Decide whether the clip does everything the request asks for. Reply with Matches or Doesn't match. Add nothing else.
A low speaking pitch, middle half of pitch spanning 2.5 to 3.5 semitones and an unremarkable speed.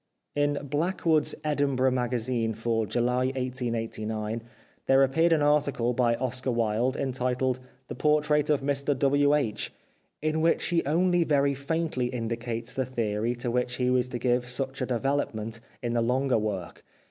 Matches